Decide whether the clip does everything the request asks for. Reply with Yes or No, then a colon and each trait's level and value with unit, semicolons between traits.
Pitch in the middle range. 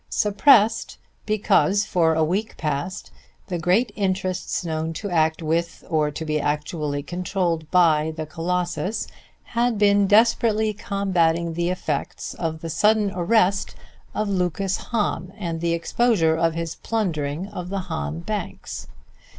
Yes: medium, 180 Hz